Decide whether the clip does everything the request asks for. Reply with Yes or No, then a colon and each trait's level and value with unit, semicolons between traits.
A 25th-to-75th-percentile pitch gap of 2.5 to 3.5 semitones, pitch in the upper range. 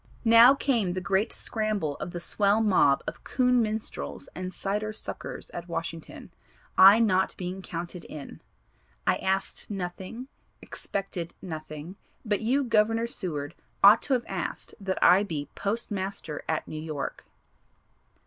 No: average, 4.0 semitones; high, 195 Hz